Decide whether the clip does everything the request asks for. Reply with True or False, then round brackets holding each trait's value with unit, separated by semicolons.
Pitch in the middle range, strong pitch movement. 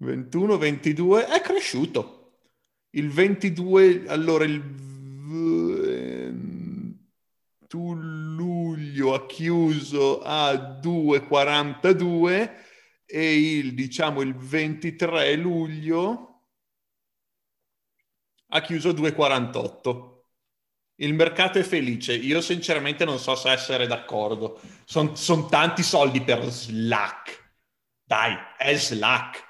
False (155 Hz; 4.2 semitones)